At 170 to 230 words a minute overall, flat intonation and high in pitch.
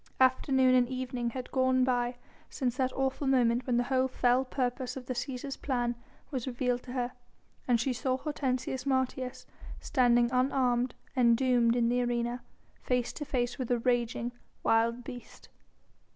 No: average, 160 wpm; narrow, 1.3 semitones; very high, 250 Hz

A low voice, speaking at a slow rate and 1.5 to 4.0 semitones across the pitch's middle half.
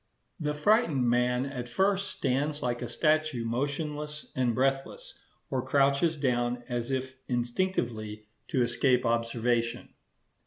Yes: low, 130 Hz; slow, 120 wpm; average, 3.6 semitones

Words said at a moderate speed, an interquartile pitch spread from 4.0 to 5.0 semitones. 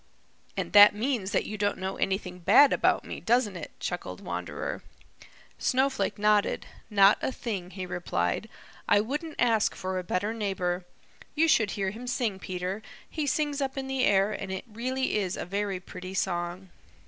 Yes: average, 170 wpm; average, 4.7 semitones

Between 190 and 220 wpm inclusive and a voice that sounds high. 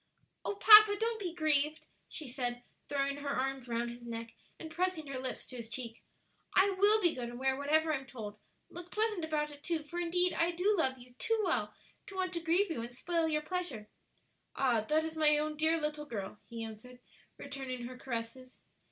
Yes: fast, 205 wpm; very high, 295 Hz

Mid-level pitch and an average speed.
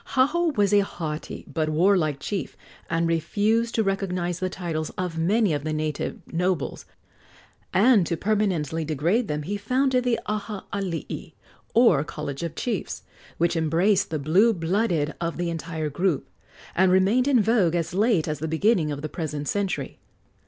Yes: medium, 180 Hz; average, 160 wpm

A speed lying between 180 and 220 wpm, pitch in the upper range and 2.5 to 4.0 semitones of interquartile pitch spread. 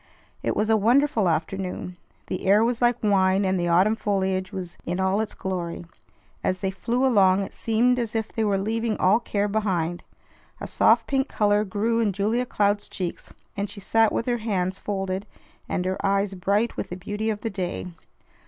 Yes: average, 190 wpm; high, 200 Hz; average, 2.8 semitones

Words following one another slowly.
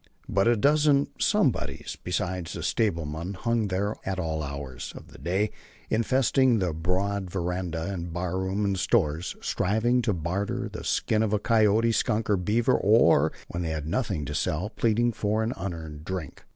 No: average, 165 wpm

